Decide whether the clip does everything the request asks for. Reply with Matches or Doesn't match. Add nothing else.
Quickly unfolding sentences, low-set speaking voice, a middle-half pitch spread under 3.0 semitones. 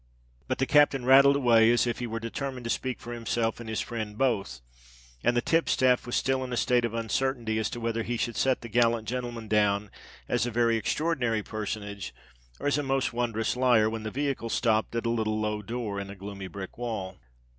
Matches